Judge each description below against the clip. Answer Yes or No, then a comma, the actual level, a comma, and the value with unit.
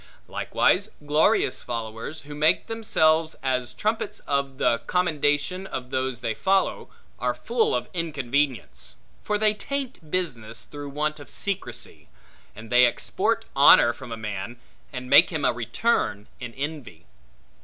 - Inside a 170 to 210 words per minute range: No, average, 140 wpm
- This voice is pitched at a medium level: Yes, medium, 145 Hz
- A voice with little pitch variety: No, wide, 5.6 semitones